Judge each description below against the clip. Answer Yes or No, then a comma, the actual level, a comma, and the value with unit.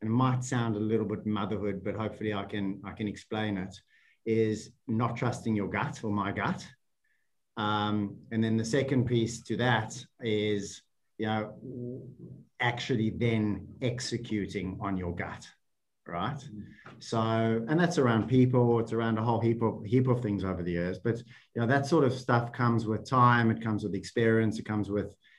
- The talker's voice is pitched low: Yes, low, 110 Hz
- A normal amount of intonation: No, narrow, 2.3 semitones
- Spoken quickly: No, average, 180 wpm